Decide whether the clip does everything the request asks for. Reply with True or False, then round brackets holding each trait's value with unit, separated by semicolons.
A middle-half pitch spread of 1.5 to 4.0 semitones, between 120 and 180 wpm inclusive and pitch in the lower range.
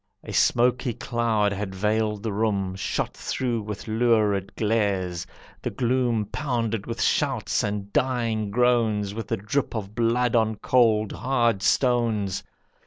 True (2.6 semitones; 135 wpm; 110 Hz)